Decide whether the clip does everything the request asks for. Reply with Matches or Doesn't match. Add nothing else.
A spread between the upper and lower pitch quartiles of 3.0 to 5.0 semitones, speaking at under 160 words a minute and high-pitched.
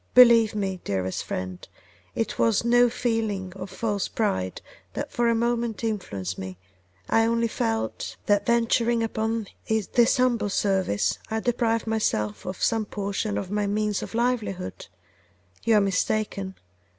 Matches